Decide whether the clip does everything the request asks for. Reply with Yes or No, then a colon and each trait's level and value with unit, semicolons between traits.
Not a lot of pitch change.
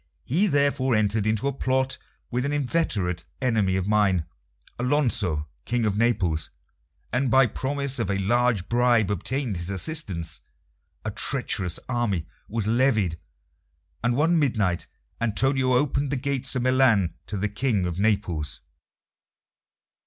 No: average, 5.2 semitones